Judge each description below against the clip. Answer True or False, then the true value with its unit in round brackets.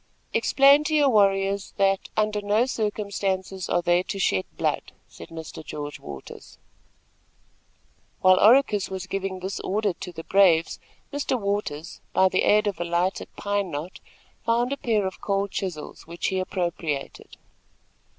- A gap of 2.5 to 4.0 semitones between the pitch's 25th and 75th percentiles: True (3.1 semitones)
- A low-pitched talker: False (195 Hz)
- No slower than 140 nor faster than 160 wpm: True (150 wpm)